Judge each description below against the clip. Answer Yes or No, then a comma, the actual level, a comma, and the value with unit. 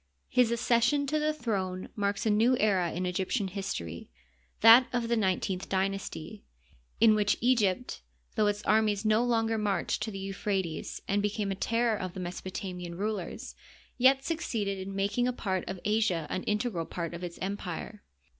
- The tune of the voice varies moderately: Yes, average, 3.4 semitones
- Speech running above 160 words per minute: Yes, average, 170 wpm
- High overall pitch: Yes, high, 205 Hz